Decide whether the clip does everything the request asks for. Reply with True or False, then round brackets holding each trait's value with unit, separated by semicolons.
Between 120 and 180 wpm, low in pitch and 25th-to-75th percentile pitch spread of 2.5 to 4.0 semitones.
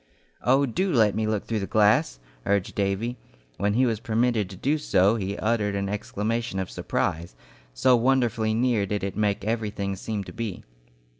True (175 wpm; 110 Hz; 2.9 semitones)